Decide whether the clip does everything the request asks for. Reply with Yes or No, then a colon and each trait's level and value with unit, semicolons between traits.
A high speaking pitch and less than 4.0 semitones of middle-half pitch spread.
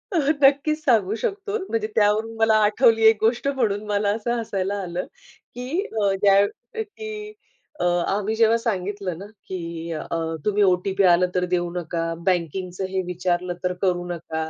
No: high, 205 Hz; average, 4.3 semitones